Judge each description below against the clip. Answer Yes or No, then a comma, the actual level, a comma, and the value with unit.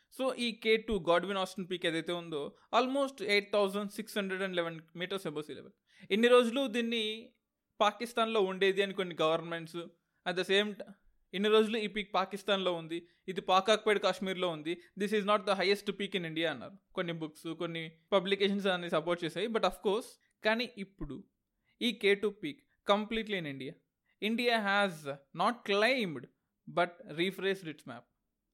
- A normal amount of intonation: Yes, average, 3.5 semitones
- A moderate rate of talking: No, fast, 165 wpm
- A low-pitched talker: No, high, 195 Hz